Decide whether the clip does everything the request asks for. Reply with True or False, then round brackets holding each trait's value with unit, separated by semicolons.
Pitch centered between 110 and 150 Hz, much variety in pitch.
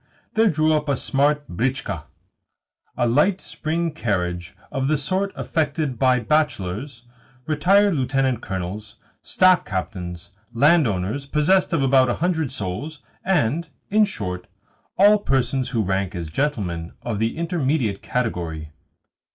True (135 Hz; 7.4 semitones)